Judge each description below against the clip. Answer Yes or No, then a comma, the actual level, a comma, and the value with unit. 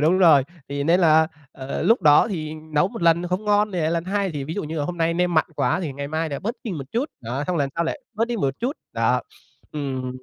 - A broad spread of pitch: No, average, 4.2 semitones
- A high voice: No, medium, 165 Hz